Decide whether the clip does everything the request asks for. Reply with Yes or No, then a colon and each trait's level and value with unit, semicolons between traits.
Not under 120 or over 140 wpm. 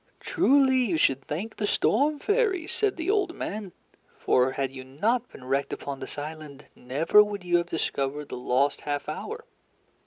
No: average, 175 wpm